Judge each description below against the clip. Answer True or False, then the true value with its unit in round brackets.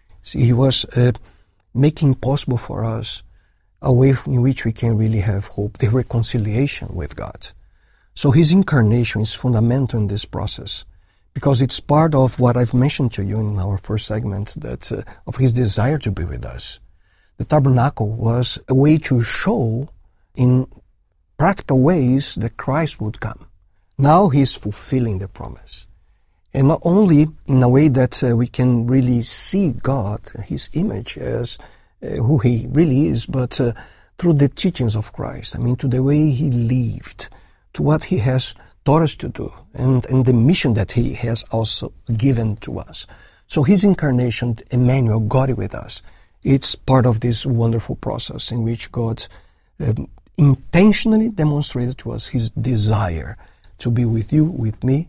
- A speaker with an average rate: True (170 wpm)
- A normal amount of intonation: True (3.9 semitones)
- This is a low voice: True (120 Hz)